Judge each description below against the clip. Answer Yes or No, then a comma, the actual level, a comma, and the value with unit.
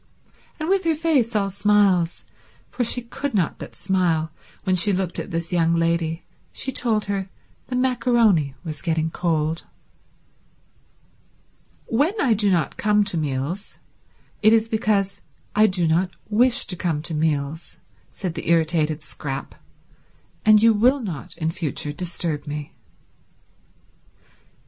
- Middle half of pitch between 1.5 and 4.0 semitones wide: No, average, 5.1 semitones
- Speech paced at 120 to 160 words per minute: Yes, average, 140 wpm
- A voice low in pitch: No, medium, 185 Hz